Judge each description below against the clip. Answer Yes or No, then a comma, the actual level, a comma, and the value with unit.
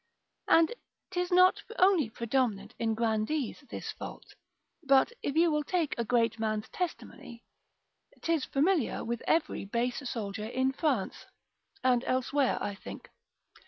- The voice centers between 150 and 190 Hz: No, very high, 255 Hz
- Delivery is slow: Yes, slow, 130 wpm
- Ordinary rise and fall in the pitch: No, wide, 5.8 semitones